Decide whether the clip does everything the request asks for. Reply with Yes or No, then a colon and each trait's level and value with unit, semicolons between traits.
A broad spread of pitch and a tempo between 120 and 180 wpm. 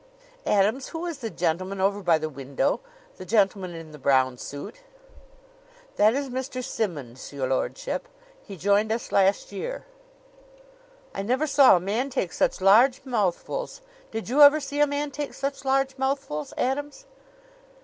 Yes: wide, 7.3 semitones; average, 155 wpm